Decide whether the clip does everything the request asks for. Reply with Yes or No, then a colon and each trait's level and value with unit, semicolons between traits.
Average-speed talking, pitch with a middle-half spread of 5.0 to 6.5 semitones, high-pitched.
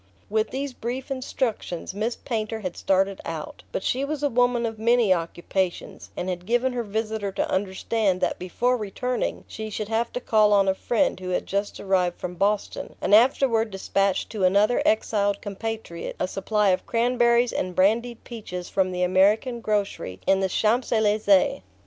No: average, 175 wpm; average, 3.7 semitones; high, 215 Hz